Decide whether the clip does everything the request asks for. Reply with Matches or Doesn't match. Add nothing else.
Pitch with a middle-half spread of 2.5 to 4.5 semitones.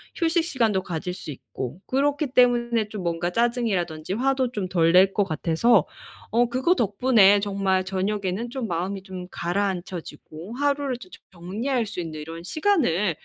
Doesn't match